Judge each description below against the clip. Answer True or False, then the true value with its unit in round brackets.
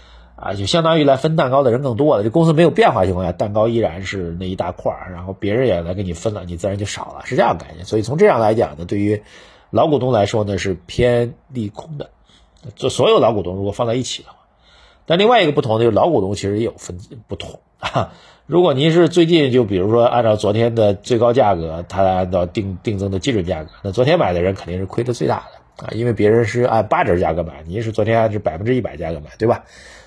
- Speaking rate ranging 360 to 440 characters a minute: True (365 characters per minute)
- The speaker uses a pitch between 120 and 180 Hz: False (110 Hz)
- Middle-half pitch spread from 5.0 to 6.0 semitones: False (4.6 semitones)